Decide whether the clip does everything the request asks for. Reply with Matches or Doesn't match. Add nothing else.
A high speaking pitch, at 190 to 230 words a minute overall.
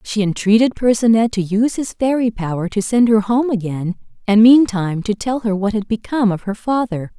Matches